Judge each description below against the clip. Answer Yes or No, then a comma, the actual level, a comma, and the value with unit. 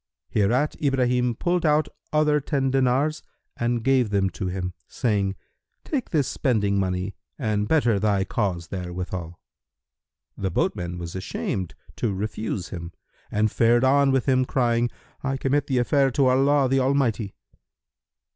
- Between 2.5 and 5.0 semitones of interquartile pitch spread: No, wide, 5.6 semitones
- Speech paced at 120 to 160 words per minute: Yes, average, 140 wpm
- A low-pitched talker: Yes, low, 120 Hz